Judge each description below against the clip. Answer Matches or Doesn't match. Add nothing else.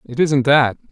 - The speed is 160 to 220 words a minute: Matches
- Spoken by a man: Matches